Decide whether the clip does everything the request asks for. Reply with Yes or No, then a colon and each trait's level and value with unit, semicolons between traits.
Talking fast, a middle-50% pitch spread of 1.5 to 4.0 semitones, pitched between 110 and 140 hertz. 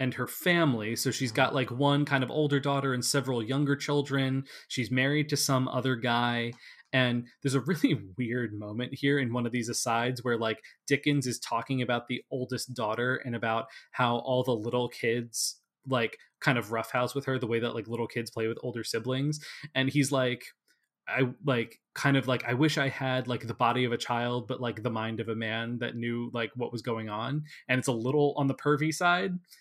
Yes: fast, 215 wpm; average, 2.7 semitones; low, 125 Hz